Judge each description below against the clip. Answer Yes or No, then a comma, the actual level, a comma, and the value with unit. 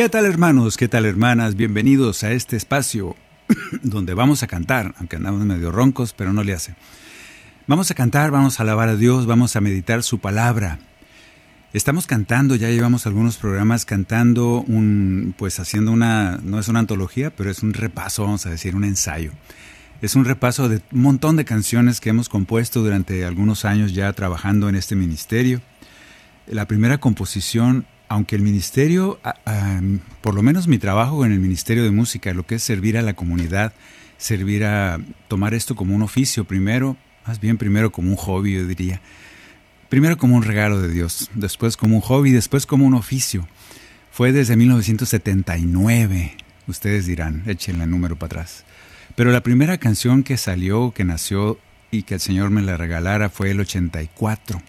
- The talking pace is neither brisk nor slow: Yes, average, 175 wpm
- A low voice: Yes, low, 105 Hz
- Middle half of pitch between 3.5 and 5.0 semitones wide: Yes, average, 3.9 semitones